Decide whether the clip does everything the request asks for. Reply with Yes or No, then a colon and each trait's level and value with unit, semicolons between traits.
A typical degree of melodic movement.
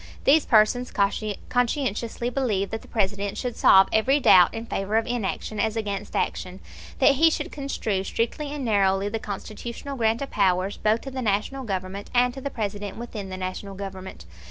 Yes: average, 3.8 semitones